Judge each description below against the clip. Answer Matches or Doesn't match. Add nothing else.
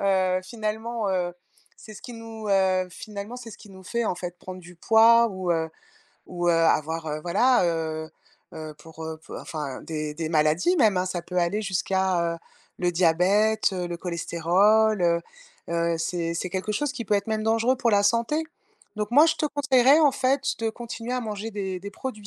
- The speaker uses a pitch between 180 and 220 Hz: Matches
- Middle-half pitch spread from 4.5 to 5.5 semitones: Matches